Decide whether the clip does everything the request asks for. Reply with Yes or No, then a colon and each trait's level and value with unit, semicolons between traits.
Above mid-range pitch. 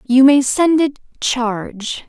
Yes: very high, 260 Hz